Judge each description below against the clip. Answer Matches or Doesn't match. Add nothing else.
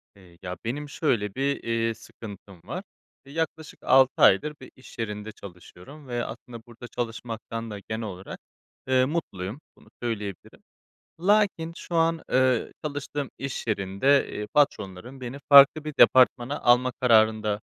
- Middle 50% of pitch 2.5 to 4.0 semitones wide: Doesn't match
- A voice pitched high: Doesn't match